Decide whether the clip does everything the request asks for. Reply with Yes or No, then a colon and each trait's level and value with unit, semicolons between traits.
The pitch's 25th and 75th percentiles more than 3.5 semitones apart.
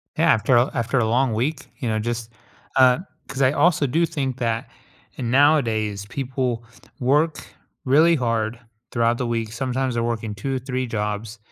No: average, 2.9 semitones